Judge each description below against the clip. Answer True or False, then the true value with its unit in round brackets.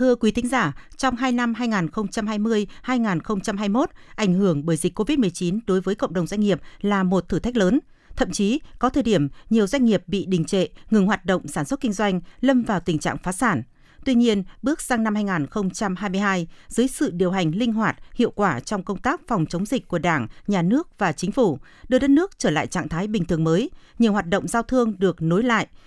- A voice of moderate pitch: False (205 Hz)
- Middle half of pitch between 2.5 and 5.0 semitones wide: True (4.6 semitones)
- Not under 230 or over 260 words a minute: False (215 wpm)